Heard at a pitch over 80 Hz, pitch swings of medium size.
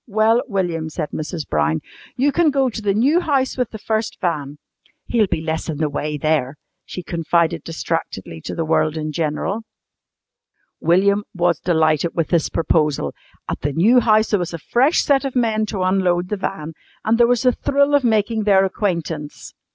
No: medium, 185 Hz; wide, 6.0 semitones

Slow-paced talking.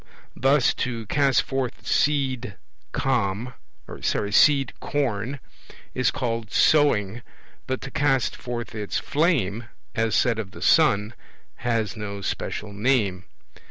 Yes: slow, 105 wpm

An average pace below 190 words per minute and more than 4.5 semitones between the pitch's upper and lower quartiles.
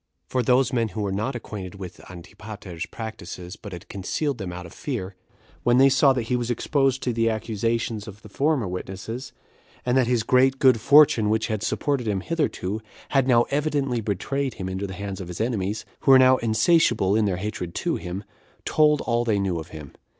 No: average, 200 wpm; average, 5.0 semitones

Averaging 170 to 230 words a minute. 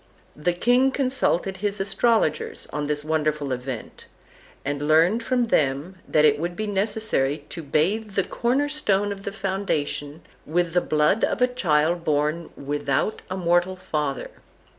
No: average, 150 wpm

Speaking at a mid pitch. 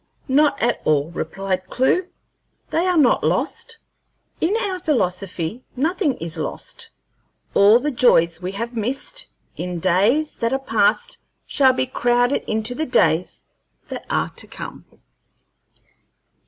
No: high, 240 Hz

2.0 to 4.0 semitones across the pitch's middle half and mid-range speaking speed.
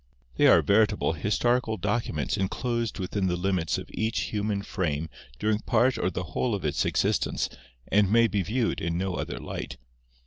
Yes: average, 3.5 semitones; average, 170 wpm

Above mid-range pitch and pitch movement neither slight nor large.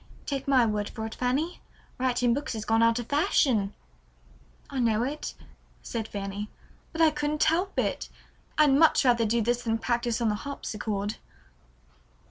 Yes: high, 240 Hz; average, 4.3 semitones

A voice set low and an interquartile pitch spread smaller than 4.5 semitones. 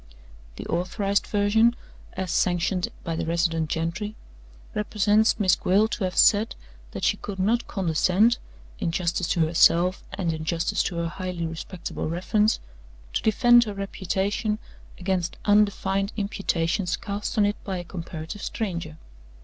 No: high, 190 Hz; average, 3.4 semitones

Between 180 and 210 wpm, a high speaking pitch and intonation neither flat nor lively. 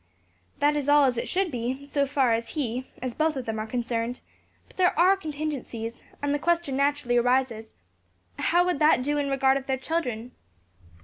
Yes: average, 190 wpm; very high, 270 Hz; average, 3.5 semitones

